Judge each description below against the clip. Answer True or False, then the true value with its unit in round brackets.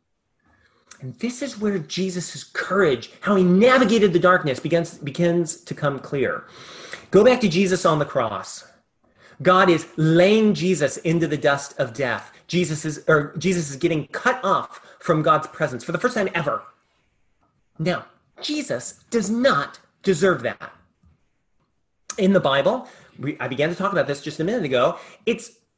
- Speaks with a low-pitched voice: False (175 Hz)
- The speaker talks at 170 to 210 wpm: False (160 wpm)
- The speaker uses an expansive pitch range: False (4.4 semitones)